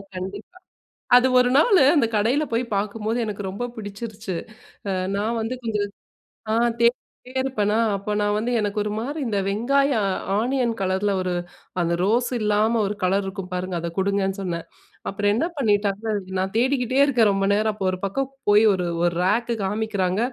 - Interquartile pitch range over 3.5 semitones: No, average, 3.2 semitones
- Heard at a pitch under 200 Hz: No, high, 210 Hz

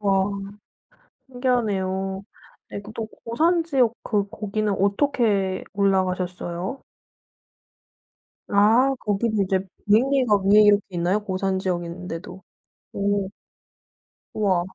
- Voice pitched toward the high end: Yes, high, 200 Hz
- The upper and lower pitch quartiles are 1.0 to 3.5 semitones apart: Yes, average, 2.9 semitones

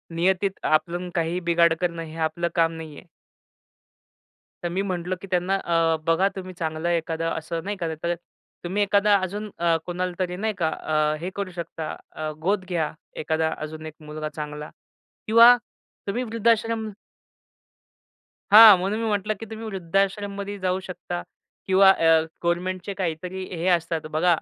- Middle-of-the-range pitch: Yes, medium, 180 Hz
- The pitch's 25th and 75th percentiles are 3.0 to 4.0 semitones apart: Yes, average, 3.3 semitones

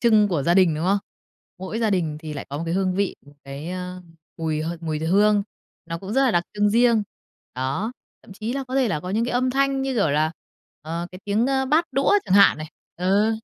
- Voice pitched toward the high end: Yes, high, 195 Hz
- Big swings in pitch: Yes, wide, 5.7 semitones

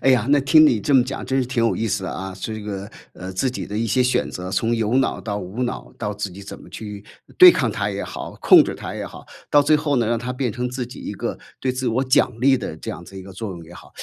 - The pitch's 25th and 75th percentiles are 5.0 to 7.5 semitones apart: No, average, 4.4 semitones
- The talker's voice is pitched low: Yes, low, 115 Hz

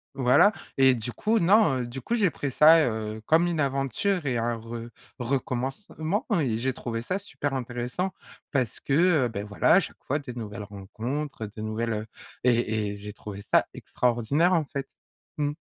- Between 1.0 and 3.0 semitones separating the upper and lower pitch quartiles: No, average, 4.7 semitones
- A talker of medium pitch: No, low, 125 Hz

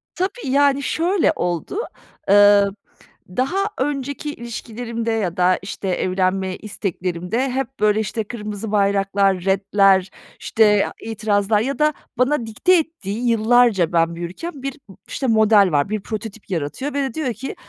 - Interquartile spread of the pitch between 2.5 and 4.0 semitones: No, average, 5.0 semitones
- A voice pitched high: Yes, high, 215 Hz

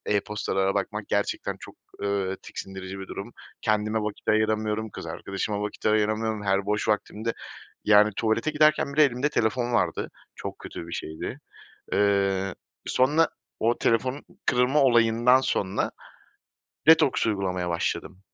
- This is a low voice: Yes, low, 110 Hz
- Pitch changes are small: No, average, 3.3 semitones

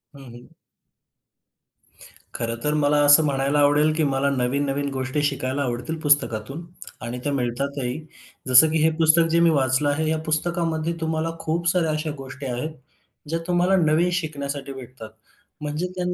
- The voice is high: No, medium, 145 Hz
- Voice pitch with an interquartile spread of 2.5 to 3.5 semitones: Yes, average, 3.0 semitones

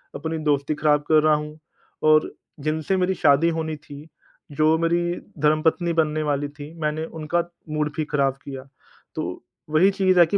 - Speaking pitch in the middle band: Yes, medium, 155 Hz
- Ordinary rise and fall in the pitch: No, narrow, 1.6 semitones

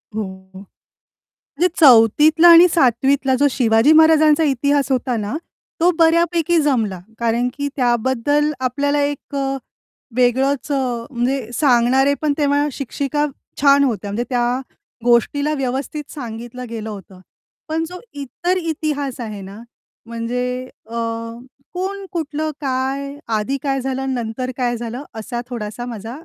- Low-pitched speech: No, very high, 265 Hz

